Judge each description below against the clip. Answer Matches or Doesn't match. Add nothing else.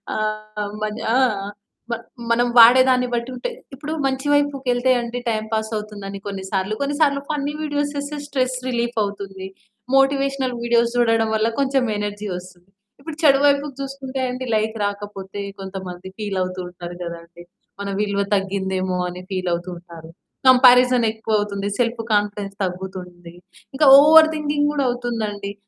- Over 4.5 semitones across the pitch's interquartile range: Matches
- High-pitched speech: Matches